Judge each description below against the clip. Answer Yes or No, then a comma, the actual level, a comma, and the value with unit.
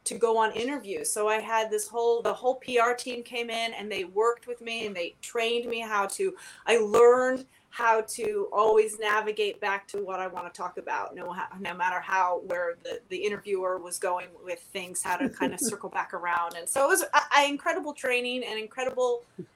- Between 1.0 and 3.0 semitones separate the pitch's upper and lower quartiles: No, average, 4.2 semitones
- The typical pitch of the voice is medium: No, high, 225 Hz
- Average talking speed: No, fast, 210 wpm